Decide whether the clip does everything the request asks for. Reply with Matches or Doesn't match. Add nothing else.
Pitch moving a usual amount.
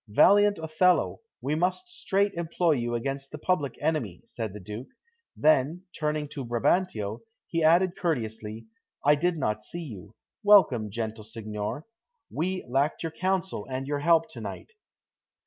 Doesn't match